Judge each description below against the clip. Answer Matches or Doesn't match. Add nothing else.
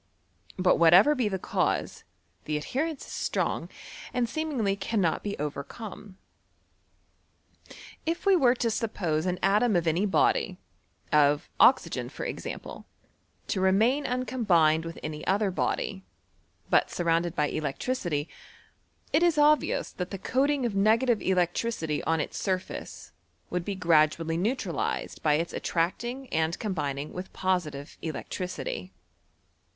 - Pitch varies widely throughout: Matches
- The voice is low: Doesn't match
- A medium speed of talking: Doesn't match